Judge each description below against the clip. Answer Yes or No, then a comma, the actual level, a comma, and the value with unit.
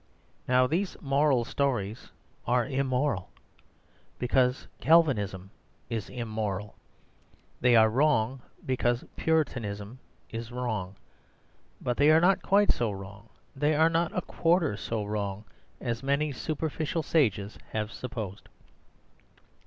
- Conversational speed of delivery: No, slow, 115 wpm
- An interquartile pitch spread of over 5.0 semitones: Yes, wide, 5.5 semitones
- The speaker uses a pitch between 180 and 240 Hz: No, low, 125 Hz